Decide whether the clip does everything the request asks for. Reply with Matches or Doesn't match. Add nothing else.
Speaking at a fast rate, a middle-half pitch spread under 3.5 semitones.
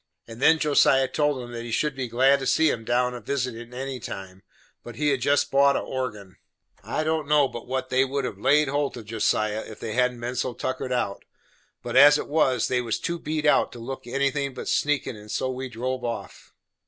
Matches